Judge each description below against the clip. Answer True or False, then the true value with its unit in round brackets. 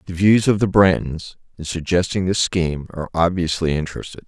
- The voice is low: True (90 Hz)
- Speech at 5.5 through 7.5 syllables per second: True (5.8 syllables/s)